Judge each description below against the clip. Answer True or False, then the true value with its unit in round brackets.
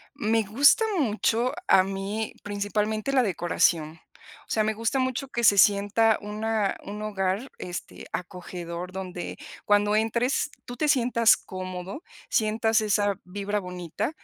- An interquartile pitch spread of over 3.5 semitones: False (2.9 semitones)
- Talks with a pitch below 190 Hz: False (210 Hz)